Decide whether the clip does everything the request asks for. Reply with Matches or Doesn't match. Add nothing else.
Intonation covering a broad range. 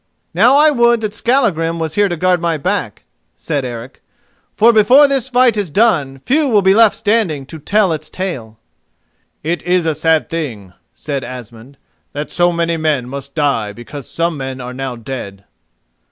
Matches